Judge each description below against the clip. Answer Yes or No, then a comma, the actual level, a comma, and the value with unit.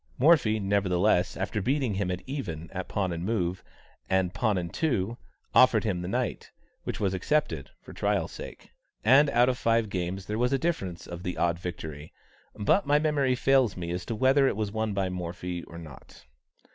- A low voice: Yes, low, 100 Hz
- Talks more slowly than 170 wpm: No, average, 190 wpm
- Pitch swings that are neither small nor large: No, wide, 5.8 semitones